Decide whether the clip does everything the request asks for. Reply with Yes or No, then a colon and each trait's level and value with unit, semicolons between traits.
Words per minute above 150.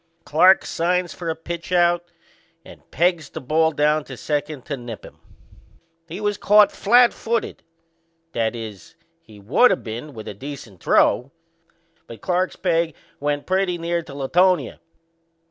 No: average, 140 wpm